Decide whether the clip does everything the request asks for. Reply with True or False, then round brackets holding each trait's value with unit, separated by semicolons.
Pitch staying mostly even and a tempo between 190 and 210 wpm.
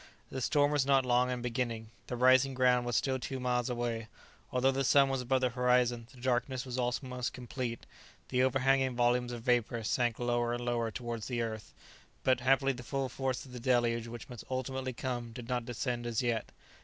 True (1.4 semitones; 200 wpm)